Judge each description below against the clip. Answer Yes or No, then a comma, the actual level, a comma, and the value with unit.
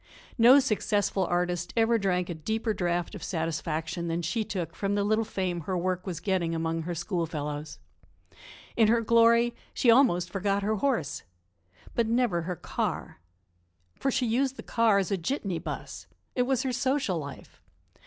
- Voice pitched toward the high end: Yes, high, 195 Hz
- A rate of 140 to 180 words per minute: Yes, average, 165 wpm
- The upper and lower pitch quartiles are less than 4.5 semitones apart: No, average, 5.0 semitones